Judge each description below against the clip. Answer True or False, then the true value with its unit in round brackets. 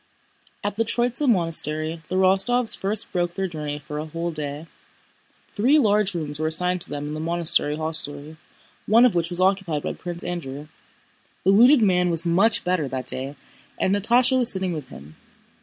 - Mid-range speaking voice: True (175 Hz)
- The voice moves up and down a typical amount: True (4.7 semitones)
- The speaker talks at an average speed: True (180 wpm)